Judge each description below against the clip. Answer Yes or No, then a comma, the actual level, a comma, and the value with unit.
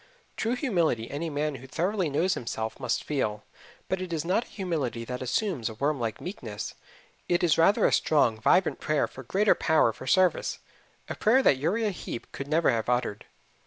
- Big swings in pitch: Yes, wide, 7.1 semitones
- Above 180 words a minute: Yes, average, 190 wpm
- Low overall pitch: No, medium, 155 Hz